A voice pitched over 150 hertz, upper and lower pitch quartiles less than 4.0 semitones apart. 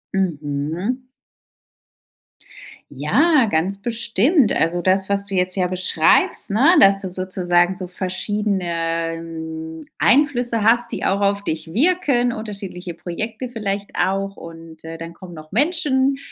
No: high, 190 Hz; average, 5.3 semitones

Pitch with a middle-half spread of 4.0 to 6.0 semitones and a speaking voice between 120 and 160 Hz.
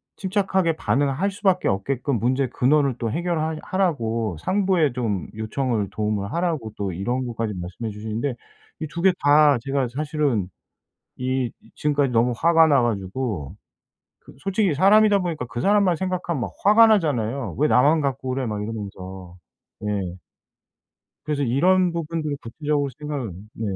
No: wide, 6.6 semitones; medium, 140 Hz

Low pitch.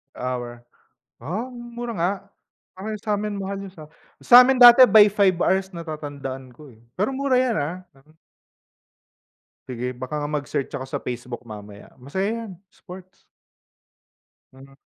No: medium, 160 Hz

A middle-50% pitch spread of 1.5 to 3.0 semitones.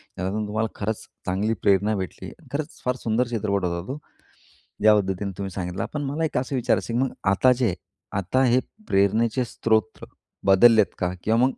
No: average, 4.2 semitones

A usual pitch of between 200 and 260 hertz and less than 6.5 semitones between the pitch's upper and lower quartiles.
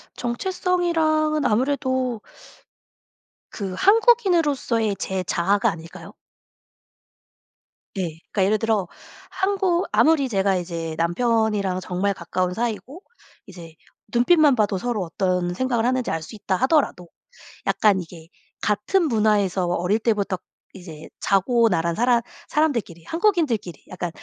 No: high, 215 Hz; wide, 7.1 semitones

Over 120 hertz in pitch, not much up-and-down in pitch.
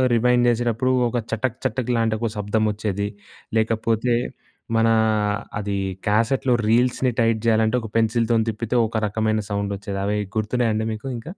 No: low, 110 Hz; narrow, 1.8 semitones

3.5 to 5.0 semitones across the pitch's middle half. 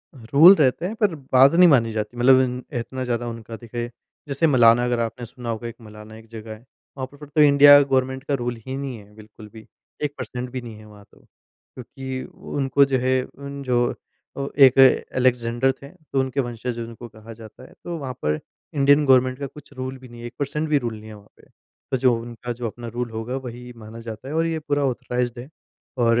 No: average, 2.9 semitones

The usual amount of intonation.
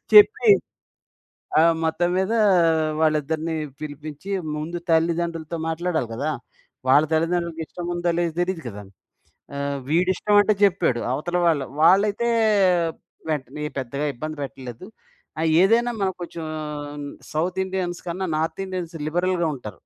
Yes: average, 3.0 semitones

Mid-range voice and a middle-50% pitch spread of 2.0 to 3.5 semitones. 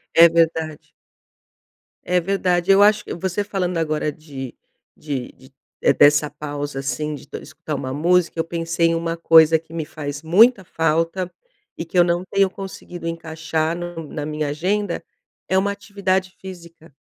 Yes: medium, 165 Hz; average, 2.9 semitones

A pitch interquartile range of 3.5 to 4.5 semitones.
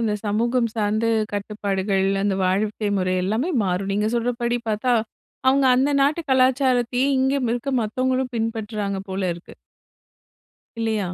Yes: average, 3.8 semitones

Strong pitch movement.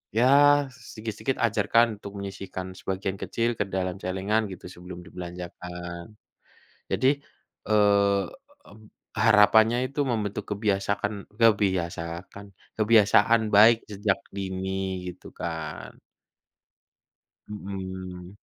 No: average, 2.9 semitones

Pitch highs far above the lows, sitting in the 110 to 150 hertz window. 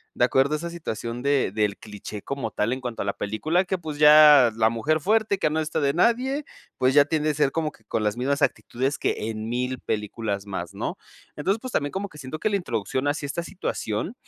Yes: wide, 5.7 semitones; medium, 140 Hz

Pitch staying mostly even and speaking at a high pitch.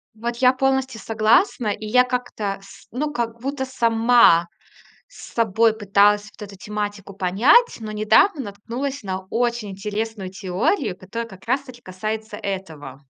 No: average, 3.8 semitones; high, 220 Hz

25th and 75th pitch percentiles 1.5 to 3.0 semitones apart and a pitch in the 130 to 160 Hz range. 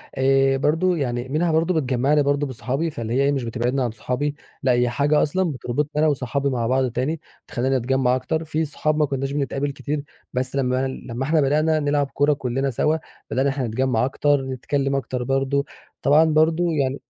Yes: narrow, 2.5 semitones; low, 135 Hz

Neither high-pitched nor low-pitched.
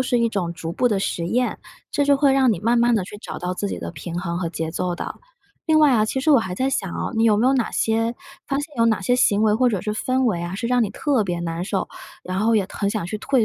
No: high, 220 Hz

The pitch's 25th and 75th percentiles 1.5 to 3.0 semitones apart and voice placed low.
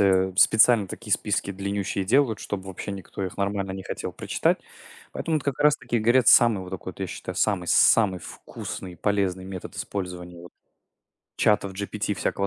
Yes: narrow, 2.4 semitones; low, 100 Hz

